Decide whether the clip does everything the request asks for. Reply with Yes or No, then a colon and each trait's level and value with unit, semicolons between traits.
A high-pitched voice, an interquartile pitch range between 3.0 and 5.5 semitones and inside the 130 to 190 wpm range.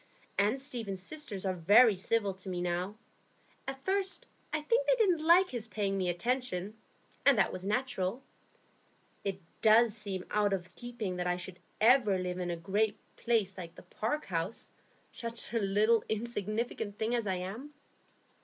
Yes: high, 210 Hz; average, 4.4 semitones; average, 165 wpm